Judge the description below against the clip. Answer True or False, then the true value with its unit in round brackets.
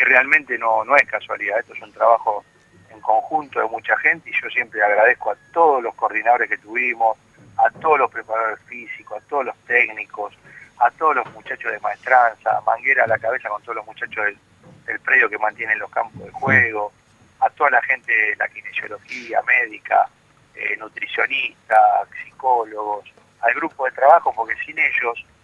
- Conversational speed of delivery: True (175 wpm)